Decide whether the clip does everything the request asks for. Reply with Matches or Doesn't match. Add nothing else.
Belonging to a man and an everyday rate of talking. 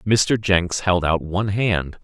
Matches